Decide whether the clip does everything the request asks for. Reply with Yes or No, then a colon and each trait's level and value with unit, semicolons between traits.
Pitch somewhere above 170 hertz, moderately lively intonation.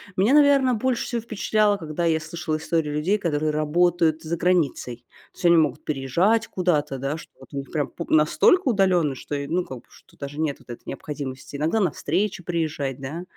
No: medium, 160 Hz; average, 4.0 semitones